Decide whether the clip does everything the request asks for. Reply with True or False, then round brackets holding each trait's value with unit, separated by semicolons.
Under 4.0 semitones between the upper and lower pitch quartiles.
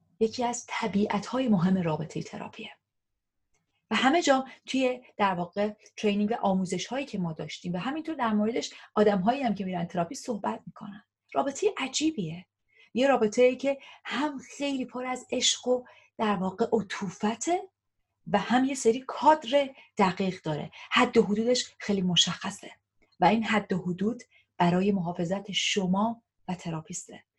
False (5.1 semitones)